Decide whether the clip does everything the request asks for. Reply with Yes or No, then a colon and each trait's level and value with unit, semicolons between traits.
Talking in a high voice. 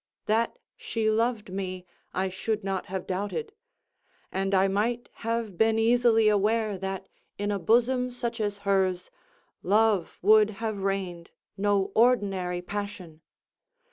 Yes: high, 205 Hz